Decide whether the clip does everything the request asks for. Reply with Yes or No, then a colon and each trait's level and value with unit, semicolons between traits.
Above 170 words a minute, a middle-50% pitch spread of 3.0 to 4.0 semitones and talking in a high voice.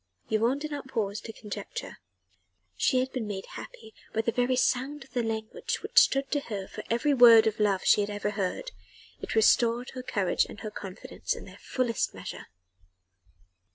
Yes: average, 185 wpm; average, 3.5 semitones; high, 225 Hz